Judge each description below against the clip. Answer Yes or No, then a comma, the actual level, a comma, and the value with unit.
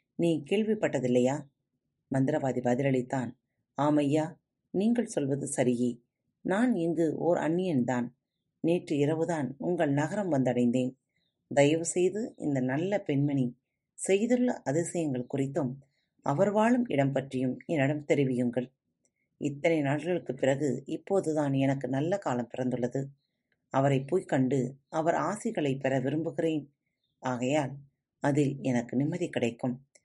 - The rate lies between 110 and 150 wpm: No, average, 100 wpm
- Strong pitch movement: No, average, 4.3 semitones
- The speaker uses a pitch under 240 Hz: Yes, medium, 140 Hz